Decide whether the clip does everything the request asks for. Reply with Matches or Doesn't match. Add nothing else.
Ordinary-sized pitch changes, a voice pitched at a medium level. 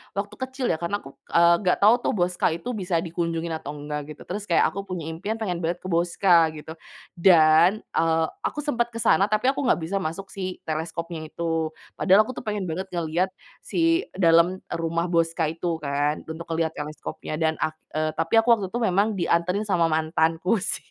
Matches